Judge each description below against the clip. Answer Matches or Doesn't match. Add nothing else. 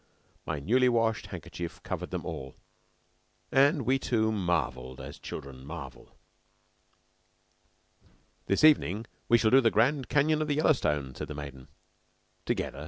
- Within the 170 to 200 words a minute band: Doesn't match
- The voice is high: Doesn't match